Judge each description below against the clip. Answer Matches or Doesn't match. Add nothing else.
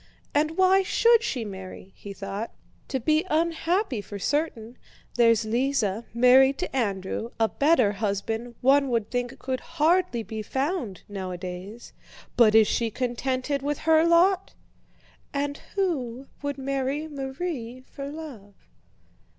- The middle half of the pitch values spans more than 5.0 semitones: Matches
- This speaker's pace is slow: Matches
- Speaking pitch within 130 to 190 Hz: Doesn't match